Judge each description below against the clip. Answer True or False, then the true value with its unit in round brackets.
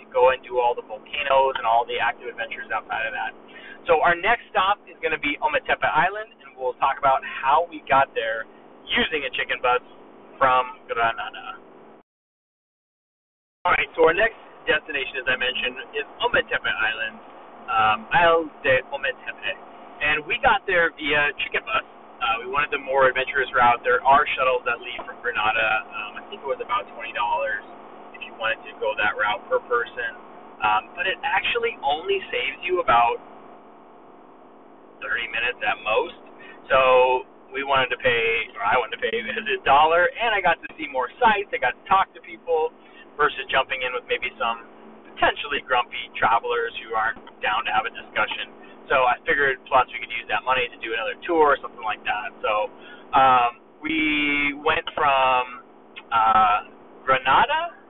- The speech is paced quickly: False (170 wpm)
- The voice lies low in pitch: False (310 Hz)